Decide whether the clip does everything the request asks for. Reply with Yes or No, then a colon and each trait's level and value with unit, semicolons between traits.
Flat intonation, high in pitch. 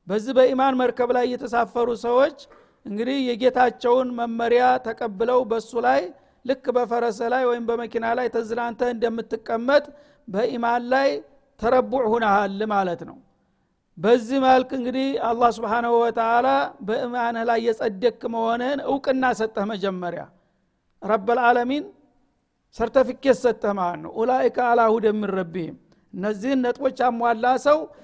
Yes: narrow, 1.9 semitones; high, 240 Hz